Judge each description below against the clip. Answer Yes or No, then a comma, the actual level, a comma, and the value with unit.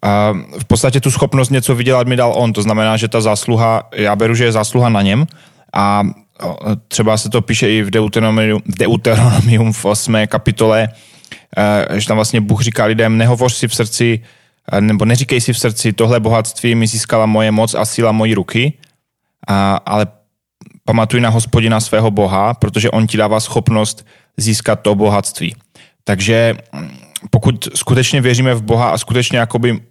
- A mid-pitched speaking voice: No, low, 115 Hz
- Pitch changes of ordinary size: No, narrow, 1.9 semitones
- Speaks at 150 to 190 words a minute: Yes, fast, 165 wpm